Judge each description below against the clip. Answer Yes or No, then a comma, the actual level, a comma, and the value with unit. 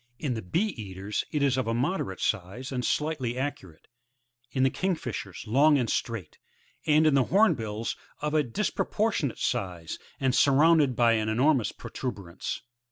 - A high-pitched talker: No, low, 130 Hz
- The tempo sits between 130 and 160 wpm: Yes, average, 155 wpm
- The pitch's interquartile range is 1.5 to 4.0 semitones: No, wide, 5.5 semitones